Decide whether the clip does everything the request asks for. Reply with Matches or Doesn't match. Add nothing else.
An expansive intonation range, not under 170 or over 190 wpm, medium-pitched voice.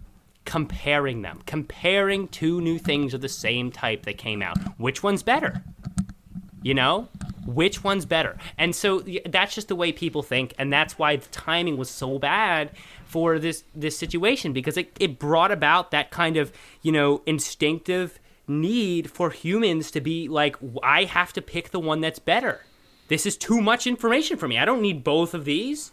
Doesn't match